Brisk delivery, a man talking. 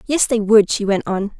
No: fast, 260 wpm; female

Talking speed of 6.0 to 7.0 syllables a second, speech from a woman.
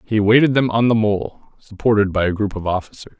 No: 6.2 syllables/s; male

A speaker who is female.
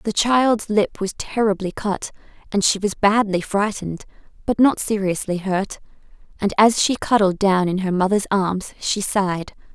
Yes: female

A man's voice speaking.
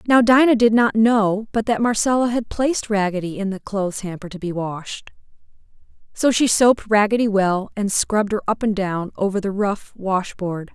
No: female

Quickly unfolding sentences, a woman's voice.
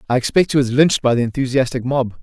No: fast, 240 wpm; male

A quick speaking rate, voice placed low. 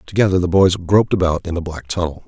Yes: fast, 235 wpm; very low, 90 Hz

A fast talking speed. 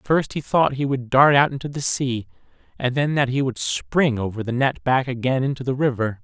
Yes: fast, 230 wpm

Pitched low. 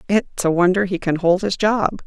No: medium, 185 Hz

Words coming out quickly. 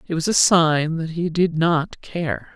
Yes: fast, 210 wpm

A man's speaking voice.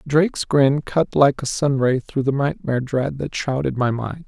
Yes: male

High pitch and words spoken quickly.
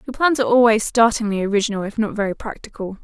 No: high, 220 Hz; average, 195 wpm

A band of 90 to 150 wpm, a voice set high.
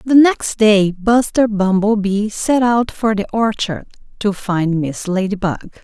Yes: average, 145 wpm; high, 210 Hz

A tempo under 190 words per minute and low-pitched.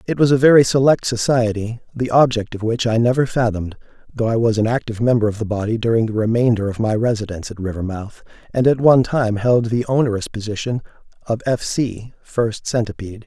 No: average, 195 wpm; low, 115 Hz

